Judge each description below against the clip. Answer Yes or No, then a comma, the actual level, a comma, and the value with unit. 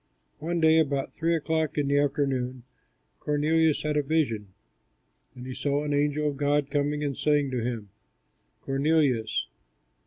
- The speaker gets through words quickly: No, average, 150 wpm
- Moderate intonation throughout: No, narrow, 2.0 semitones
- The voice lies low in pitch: No, medium, 145 Hz